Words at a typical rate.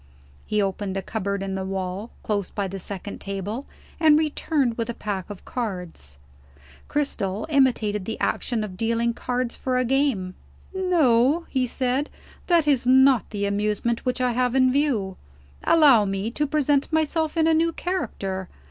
Yes: average, 165 wpm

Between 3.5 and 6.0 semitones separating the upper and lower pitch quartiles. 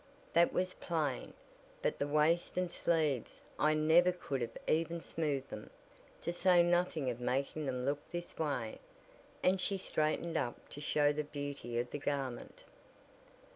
Yes: average, 3.9 semitones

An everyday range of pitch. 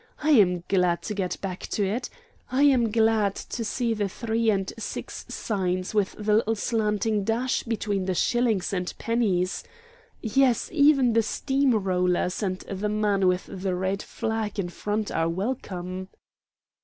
Yes: average, 3.4 semitones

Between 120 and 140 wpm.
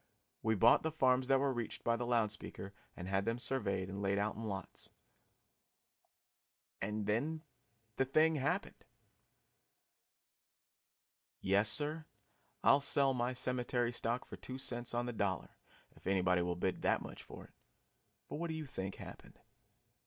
No: average, 155 wpm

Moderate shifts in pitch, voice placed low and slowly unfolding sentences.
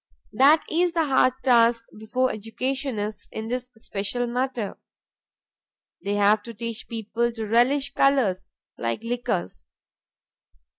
No: average, 3.1 semitones; high, 235 Hz; slow, 115 wpm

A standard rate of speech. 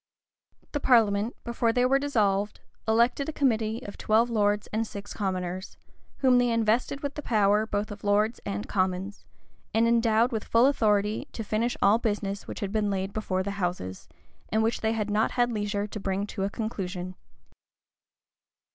Yes: average, 175 wpm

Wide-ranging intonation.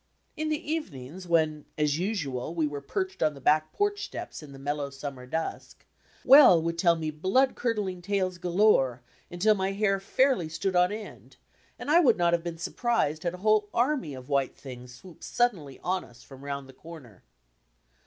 Yes: wide, 6.4 semitones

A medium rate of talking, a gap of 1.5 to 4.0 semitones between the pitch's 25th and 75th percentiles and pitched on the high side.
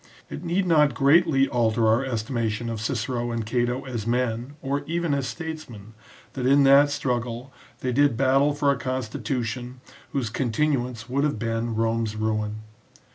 No: average, 175 wpm; average, 3.5 semitones; low, 125 Hz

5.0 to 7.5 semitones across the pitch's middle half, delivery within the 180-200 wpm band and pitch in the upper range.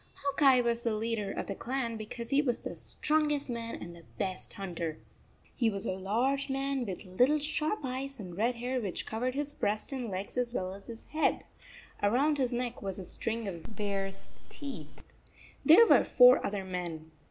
Yes: wide, 5.4 semitones; average, 195 wpm; high, 235 Hz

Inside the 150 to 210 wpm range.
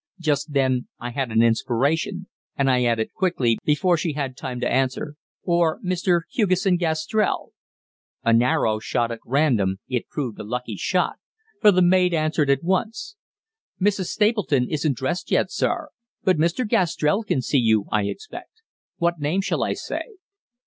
Yes: average, 160 wpm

